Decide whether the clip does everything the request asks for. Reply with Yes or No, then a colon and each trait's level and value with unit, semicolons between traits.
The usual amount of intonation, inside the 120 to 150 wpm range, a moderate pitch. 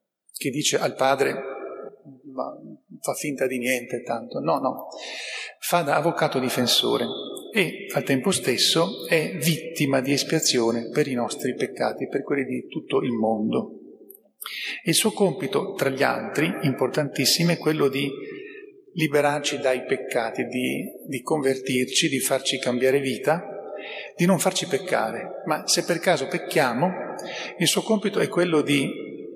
Yes: average, 4.9 semitones; average, 140 wpm; medium, 145 Hz